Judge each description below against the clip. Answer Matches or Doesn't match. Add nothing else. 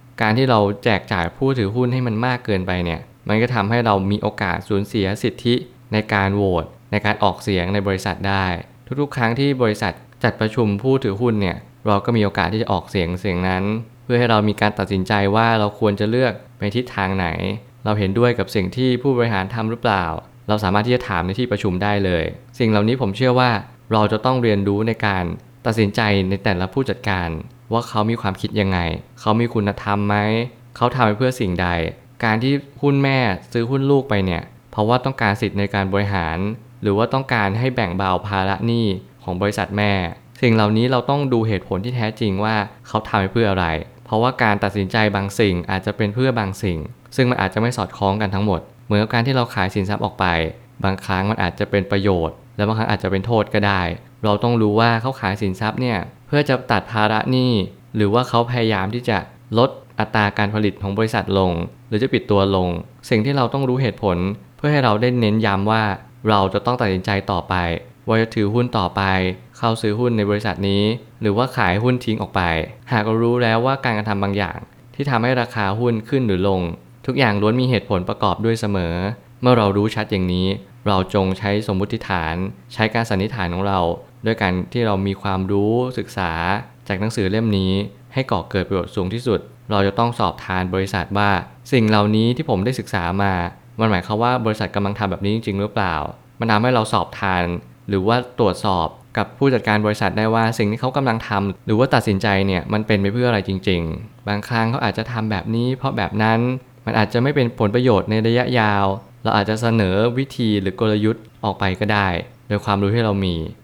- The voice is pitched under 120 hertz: Matches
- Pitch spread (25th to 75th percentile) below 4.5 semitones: Matches